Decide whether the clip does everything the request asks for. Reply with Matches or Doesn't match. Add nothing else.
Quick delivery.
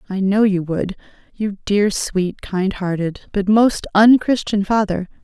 Doesn't match